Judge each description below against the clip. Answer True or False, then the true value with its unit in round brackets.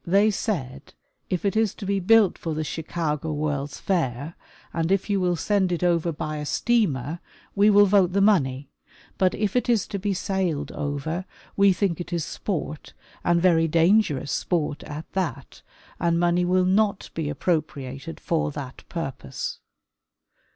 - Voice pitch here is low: False (170 Hz)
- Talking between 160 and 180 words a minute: True (165 wpm)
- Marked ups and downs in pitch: False (4.5 semitones)